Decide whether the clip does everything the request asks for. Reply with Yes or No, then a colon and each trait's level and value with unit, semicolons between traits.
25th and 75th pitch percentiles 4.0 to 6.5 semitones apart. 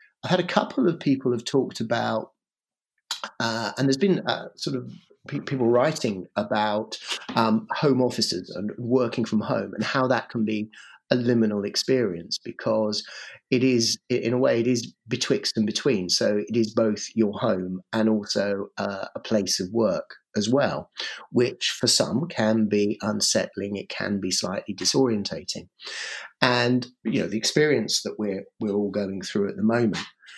No: average, 3.2 semitones